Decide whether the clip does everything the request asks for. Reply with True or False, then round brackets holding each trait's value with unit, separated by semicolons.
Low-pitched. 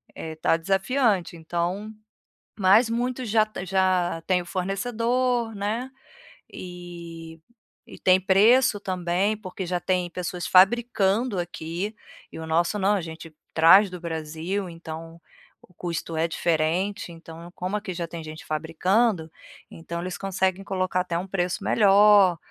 False (185 Hz)